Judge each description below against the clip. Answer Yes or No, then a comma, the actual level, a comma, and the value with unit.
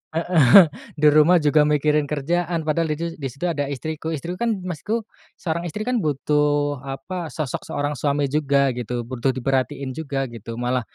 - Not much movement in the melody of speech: No, average, 3.2 semitones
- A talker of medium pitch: Yes, medium, 150 Hz